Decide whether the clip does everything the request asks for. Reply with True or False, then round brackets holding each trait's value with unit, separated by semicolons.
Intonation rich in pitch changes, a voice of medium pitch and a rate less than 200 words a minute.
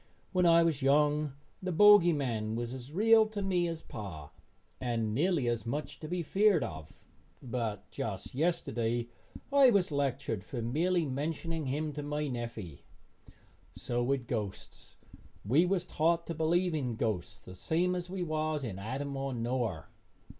True (6.2 semitones; 145 Hz; 160 wpm)